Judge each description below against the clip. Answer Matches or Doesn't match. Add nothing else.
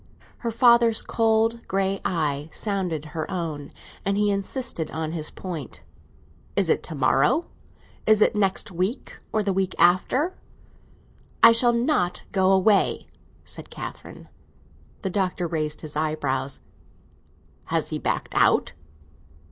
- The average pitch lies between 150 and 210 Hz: Matches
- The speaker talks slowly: Matches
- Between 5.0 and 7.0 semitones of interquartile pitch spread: Matches